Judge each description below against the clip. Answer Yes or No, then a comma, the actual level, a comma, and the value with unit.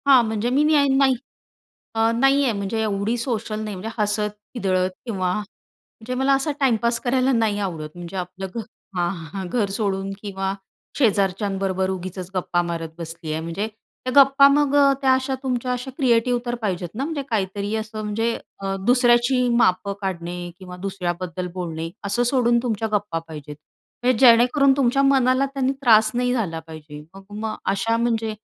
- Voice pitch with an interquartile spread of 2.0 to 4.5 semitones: No, average, 4.9 semitones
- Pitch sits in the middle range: No, high, 215 Hz